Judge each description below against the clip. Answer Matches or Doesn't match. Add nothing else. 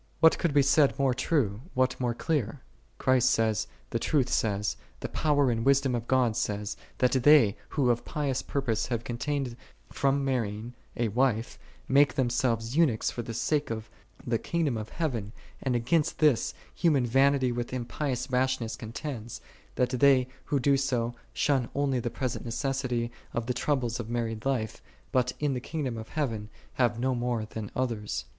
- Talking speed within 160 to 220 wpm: Matches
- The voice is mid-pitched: Doesn't match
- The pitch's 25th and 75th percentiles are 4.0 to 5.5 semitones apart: Doesn't match